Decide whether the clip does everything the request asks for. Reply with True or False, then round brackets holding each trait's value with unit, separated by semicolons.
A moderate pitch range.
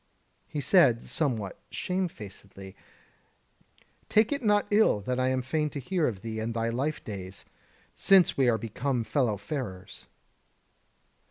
False (6.0 semitones)